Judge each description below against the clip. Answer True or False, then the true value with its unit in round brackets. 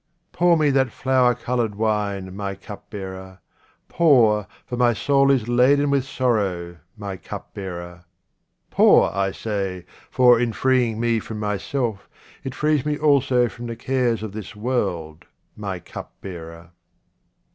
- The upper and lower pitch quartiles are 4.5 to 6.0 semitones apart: True (4.8 semitones)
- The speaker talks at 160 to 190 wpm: False (135 wpm)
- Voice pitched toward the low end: True (110 Hz)